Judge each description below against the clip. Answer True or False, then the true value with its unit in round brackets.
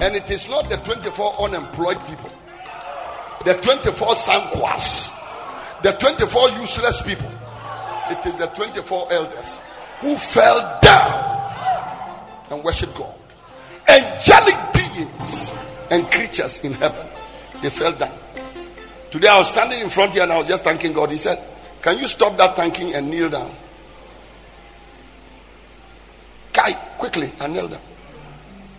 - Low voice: False (185 Hz)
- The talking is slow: True (130 wpm)